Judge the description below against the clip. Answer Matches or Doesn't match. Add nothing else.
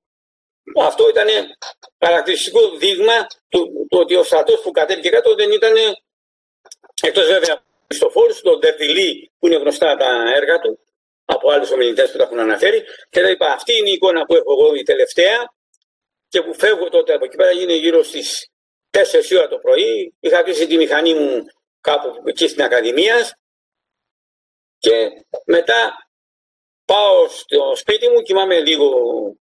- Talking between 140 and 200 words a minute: Matches